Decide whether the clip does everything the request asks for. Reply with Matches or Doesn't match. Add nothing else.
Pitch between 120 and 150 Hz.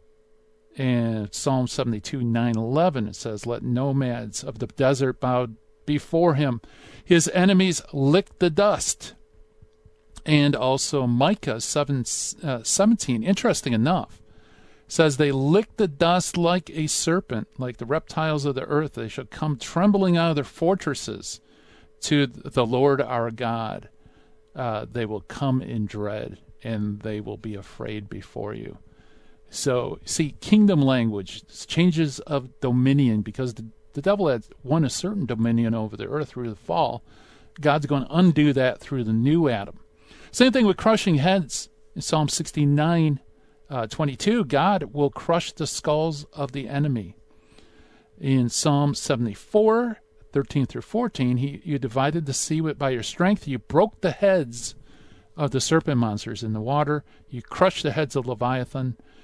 Matches